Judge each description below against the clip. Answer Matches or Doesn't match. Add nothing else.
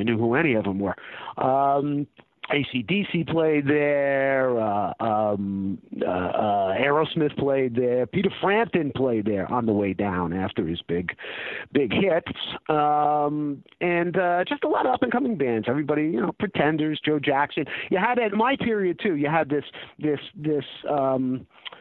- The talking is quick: Doesn't match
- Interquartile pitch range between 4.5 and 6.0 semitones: Matches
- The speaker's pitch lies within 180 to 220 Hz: Doesn't match